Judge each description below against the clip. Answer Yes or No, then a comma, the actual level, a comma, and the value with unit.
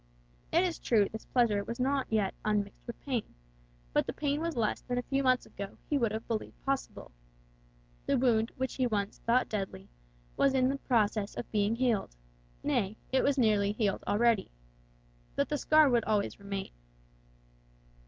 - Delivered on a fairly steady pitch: No, average, 4.0 semitones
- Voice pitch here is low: No, high, 230 Hz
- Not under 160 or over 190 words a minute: Yes, average, 170 wpm